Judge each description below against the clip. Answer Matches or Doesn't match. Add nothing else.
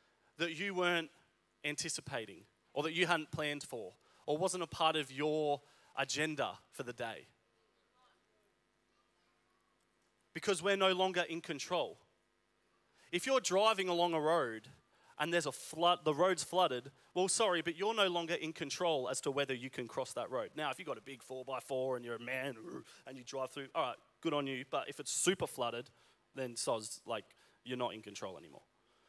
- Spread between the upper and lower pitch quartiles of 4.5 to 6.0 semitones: Matches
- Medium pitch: Matches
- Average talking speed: Matches